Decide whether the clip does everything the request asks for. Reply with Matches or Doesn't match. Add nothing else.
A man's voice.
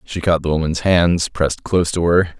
Matches